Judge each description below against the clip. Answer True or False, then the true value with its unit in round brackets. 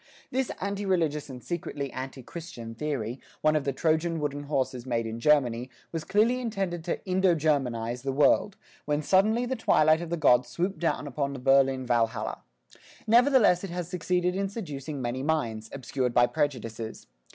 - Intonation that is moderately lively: False (5.7 semitones)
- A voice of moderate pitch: True (150 Hz)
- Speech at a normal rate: True (170 wpm)